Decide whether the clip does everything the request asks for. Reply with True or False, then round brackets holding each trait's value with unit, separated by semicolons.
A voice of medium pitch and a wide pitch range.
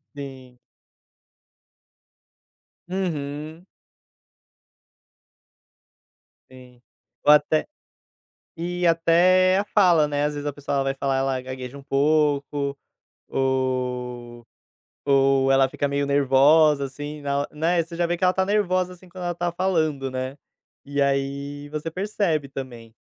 False (145 Hz; 3.8 semitones)